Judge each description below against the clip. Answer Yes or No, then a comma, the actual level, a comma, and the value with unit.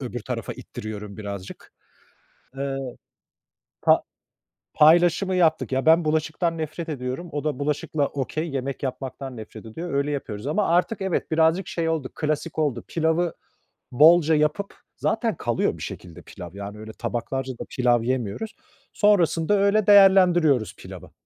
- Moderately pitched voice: Yes, medium, 150 Hz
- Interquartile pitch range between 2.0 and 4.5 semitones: No, average, 5.0 semitones